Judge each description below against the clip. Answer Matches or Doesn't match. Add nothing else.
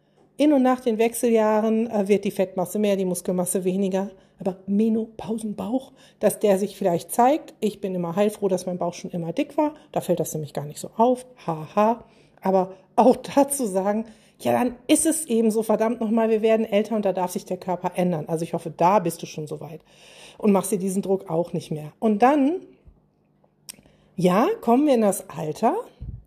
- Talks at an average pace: Doesn't match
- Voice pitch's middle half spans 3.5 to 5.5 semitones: Matches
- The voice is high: Matches